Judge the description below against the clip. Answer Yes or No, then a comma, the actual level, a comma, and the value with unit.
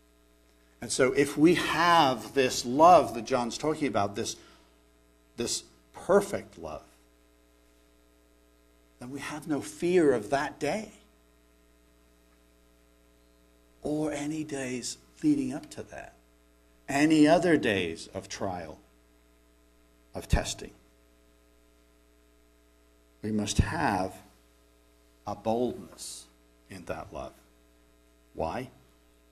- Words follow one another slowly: Yes, slow, 95 wpm